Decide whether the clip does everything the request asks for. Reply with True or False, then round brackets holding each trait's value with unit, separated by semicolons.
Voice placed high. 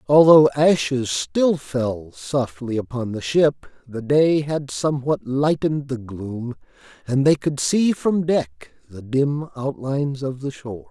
False (140 Hz)